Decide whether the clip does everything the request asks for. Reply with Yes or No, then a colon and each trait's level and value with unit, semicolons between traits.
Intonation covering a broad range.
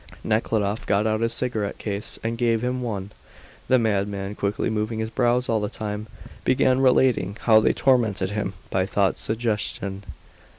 No: narrow, 2.5 semitones